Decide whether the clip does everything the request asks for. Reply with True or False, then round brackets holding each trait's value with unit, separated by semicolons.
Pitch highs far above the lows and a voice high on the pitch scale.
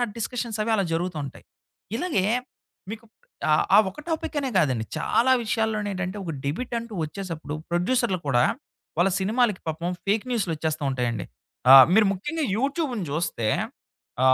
True (6.2 semitones; 195 Hz)